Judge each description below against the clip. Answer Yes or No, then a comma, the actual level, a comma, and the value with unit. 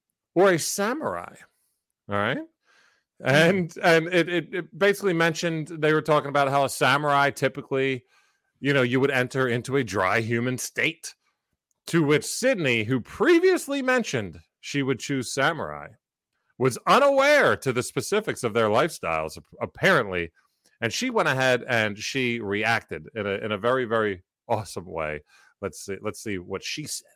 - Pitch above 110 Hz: Yes, low, 135 Hz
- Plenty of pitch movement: Yes, wide, 6.4 semitones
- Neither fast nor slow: Yes, average, 155 wpm